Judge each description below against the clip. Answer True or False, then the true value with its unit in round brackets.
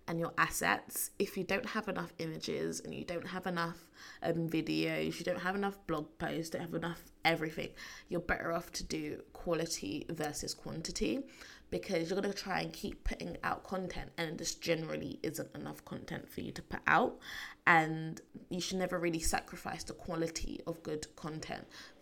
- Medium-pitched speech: True (170 Hz)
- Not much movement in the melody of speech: True (2.2 semitones)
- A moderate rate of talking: True (175 wpm)